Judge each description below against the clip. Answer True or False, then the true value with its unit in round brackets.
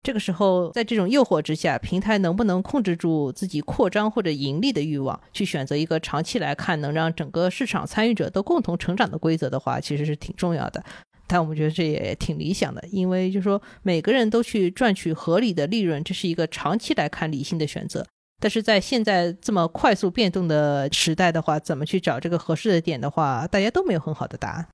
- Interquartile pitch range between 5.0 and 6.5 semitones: False (4.3 semitones)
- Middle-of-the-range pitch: True (175 Hz)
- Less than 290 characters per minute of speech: False (350 characters per minute)